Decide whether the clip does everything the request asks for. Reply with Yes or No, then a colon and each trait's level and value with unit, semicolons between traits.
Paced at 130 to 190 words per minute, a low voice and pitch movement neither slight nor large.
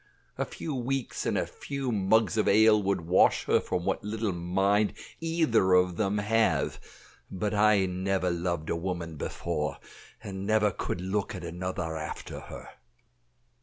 Yes: average, 155 wpm; very low, 95 Hz; average, 3.2 semitones